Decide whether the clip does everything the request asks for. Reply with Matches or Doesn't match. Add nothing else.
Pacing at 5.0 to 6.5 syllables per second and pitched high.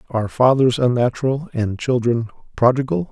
Doesn't match